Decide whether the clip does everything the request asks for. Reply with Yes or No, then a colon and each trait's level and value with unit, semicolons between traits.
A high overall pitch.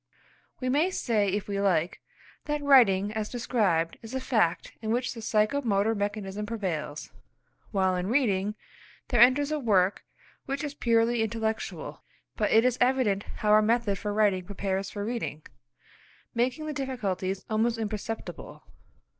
Yes: high, 220 Hz